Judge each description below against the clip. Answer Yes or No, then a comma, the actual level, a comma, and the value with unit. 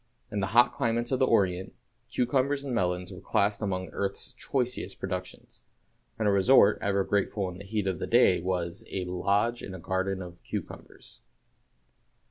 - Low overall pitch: Yes, low, 100 Hz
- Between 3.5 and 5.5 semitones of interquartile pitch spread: Yes, average, 4.1 semitones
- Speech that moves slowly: No, average, 170 wpm